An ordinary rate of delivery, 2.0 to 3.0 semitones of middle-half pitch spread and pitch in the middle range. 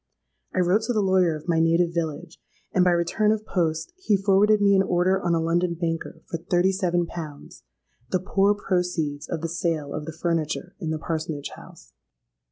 Yes: average, 185 wpm; narrow, 2.6 semitones; medium, 175 Hz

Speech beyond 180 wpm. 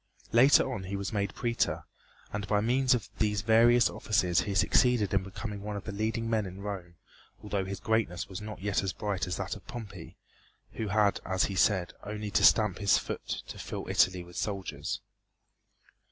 Yes: average, 190 wpm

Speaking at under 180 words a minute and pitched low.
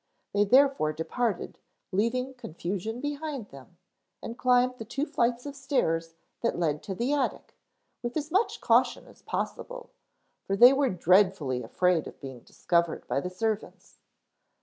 No: average, 150 wpm; high, 225 Hz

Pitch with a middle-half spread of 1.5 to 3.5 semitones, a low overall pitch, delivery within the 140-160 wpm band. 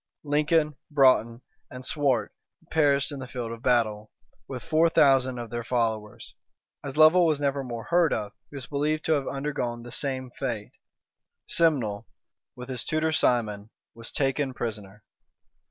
No: average, 3.9 semitones; low, 130 Hz; average, 155 wpm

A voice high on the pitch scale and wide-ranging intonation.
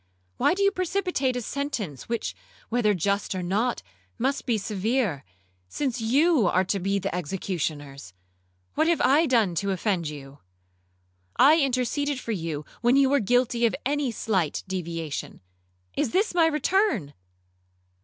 Yes: high, 225 Hz; wide, 7.9 semitones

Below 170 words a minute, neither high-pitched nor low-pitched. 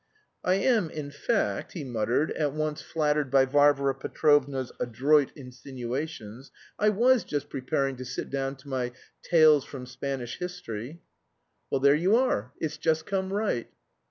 Yes: average, 150 wpm; medium, 145 Hz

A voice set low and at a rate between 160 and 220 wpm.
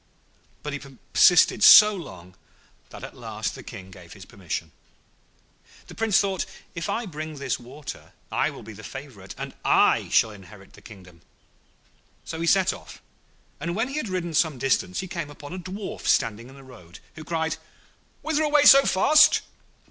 No: medium, 150 Hz; average, 175 wpm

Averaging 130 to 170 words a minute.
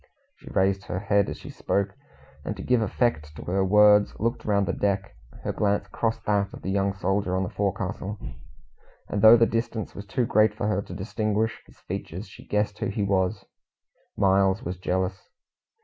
No: average, 190 wpm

